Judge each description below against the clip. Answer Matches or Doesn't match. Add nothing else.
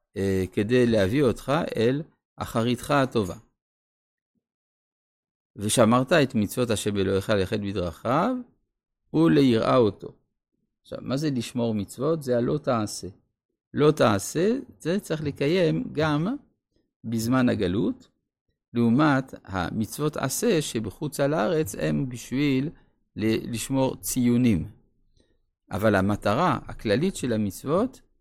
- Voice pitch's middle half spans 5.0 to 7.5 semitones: Matches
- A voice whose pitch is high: Doesn't match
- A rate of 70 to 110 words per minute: Matches